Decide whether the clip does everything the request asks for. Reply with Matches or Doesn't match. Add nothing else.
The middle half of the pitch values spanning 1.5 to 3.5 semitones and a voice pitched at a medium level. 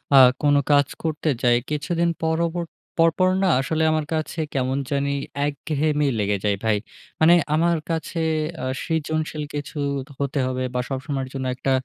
Matches